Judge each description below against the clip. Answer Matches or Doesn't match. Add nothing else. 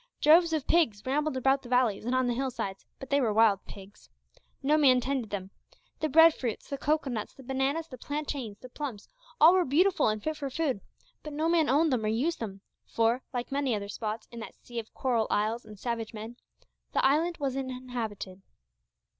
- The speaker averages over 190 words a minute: Matches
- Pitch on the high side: Matches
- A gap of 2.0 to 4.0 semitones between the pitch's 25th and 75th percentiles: Doesn't match